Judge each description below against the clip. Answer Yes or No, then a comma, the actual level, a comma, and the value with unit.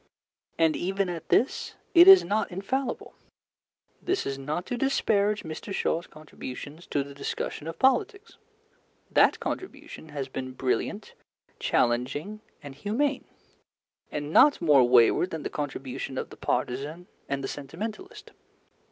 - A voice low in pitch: No, medium, 160 Hz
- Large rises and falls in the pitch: Yes, wide, 7.7 semitones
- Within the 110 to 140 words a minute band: Yes, slow, 135 wpm